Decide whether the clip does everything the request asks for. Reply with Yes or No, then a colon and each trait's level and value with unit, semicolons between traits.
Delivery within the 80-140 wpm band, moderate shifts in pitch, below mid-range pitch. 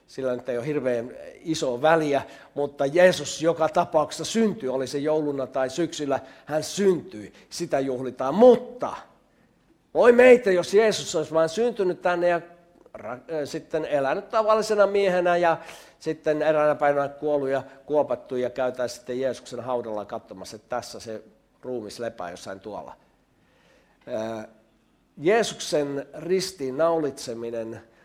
No: average, 125 wpm; average, 4.7 semitones; medium, 150 Hz